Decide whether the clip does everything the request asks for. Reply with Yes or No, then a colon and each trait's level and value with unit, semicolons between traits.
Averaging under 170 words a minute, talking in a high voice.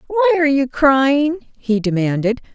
Yes: average, 140 wpm; very high, 250 Hz